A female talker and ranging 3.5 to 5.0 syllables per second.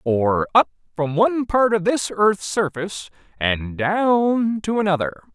No: male; 4.0 syllables/s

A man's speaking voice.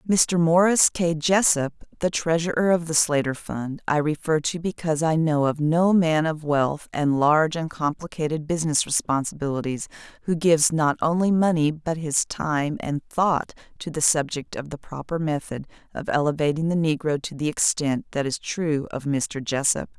No: female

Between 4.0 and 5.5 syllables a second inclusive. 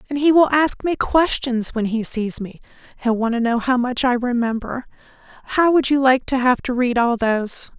Yes: 5.2 syllables/s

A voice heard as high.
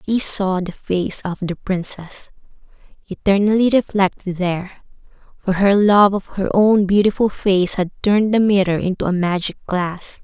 Yes: high, 195 Hz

